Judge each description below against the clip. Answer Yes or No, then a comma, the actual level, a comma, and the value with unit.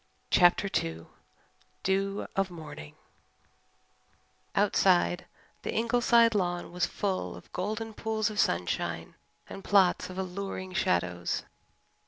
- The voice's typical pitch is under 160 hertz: No, medium, 185 Hz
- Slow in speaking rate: Yes, slow, 105 wpm